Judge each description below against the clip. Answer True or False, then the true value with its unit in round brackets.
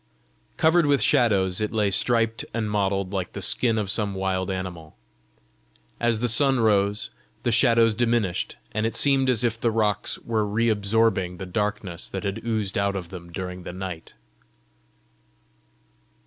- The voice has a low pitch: True (105 Hz)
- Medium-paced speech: True (160 wpm)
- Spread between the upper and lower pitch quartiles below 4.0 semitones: True (3.3 semitones)